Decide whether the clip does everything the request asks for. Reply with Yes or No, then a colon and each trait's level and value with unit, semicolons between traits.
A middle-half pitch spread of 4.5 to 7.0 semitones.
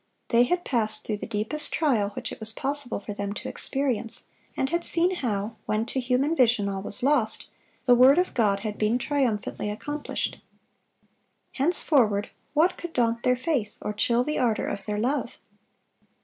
Yes: average, 5.1 semitones